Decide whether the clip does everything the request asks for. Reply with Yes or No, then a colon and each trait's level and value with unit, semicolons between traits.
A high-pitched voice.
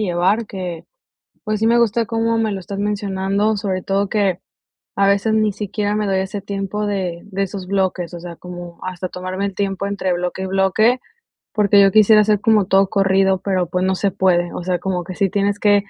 Yes: high, 195 Hz